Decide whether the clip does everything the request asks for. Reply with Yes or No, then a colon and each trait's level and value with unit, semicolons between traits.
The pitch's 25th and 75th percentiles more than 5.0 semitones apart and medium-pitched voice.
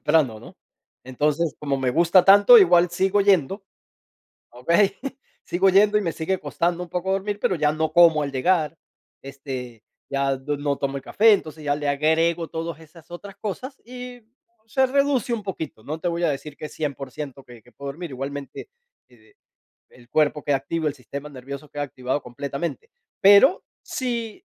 Yes: wide, 5.4 semitones; medium, 160 Hz